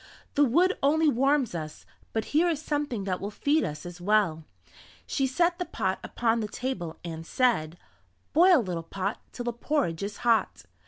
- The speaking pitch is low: No, high, 230 Hz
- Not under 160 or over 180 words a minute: Yes, average, 175 wpm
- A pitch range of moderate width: No, wide, 8.4 semitones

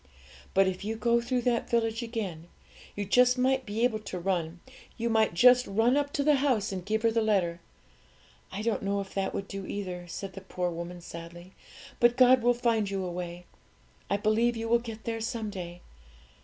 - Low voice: No, high, 215 Hz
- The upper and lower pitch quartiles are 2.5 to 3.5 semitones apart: No, average, 4.0 semitones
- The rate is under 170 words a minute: No, average, 175 wpm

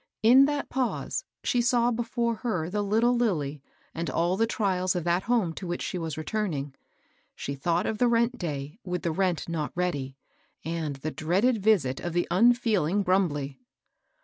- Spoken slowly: No, average, 175 wpm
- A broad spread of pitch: Yes, wide, 6.1 semitones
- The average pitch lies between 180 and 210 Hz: Yes, medium, 185 Hz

